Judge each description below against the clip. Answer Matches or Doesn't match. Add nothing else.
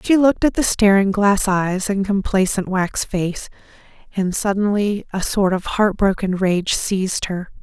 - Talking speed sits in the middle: Matches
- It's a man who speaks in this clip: Doesn't match